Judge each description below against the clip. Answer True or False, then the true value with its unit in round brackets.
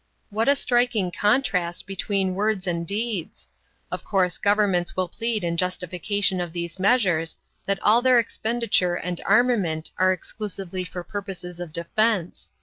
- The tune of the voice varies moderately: True (3.5 semitones)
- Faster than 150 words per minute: False (145 wpm)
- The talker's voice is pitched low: False (190 Hz)